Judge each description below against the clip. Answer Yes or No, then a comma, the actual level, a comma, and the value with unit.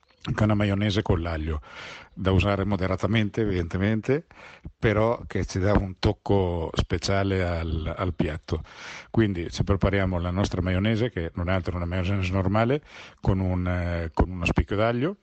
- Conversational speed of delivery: Yes, average, 160 wpm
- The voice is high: No, very low, 95 Hz